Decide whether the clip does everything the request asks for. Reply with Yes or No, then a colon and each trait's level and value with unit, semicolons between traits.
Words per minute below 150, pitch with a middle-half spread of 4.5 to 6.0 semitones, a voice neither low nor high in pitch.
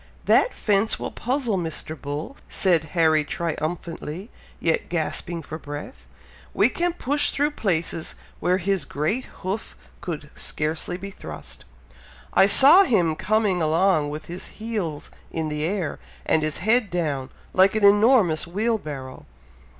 Yes: average, 140 wpm; average, 5.2 semitones; medium, 175 Hz